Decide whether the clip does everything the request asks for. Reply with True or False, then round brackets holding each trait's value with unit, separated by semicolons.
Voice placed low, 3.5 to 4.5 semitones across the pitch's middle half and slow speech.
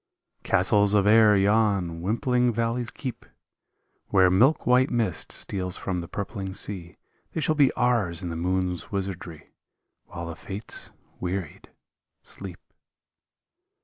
True (100 Hz; 4.2 semitones; 125 wpm)